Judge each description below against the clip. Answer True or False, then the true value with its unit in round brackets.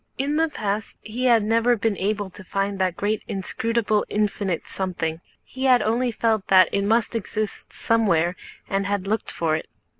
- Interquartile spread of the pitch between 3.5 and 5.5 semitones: False (2.8 semitones)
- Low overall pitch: False (210 Hz)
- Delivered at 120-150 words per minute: False (175 wpm)